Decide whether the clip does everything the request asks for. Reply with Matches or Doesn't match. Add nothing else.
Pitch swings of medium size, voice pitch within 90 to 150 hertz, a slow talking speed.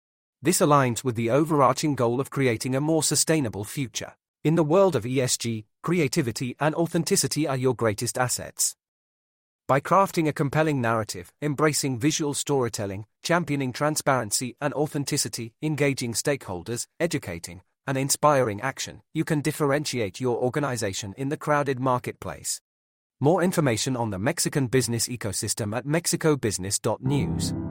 Matches